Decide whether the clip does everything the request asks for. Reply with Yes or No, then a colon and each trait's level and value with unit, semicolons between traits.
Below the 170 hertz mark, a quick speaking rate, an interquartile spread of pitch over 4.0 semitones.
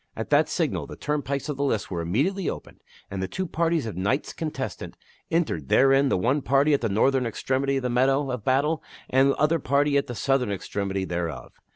Yes: low, 135 Hz; fast, 210 wpm; average, 4.8 semitones